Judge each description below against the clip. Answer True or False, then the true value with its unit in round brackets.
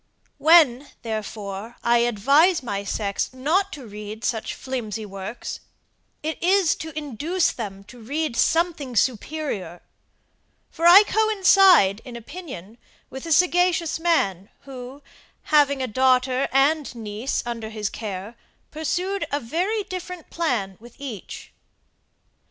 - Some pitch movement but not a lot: False (6.9 semitones)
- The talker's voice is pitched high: True (260 Hz)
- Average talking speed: False (125 wpm)